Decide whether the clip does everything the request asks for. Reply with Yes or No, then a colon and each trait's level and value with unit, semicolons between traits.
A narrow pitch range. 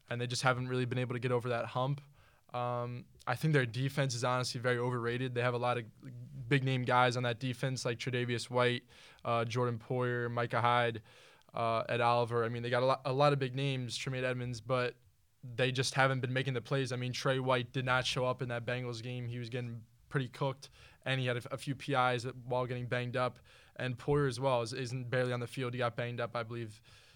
Yes: narrow, 1.3 semitones